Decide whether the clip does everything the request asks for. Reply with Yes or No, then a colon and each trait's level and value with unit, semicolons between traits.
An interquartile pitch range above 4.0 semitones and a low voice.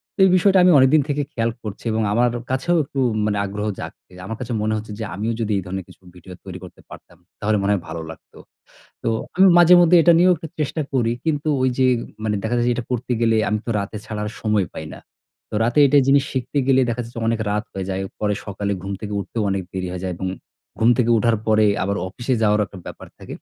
Yes: average, 4.4 semitones; low, 110 Hz